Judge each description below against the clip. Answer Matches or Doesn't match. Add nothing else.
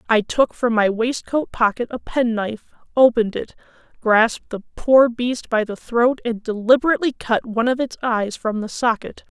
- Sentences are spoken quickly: Doesn't match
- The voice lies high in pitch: Matches